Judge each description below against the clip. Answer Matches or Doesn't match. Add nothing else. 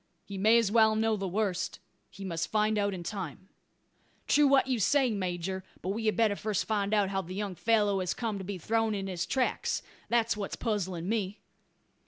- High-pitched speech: Matches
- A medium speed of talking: Doesn't match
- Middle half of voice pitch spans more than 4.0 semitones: Doesn't match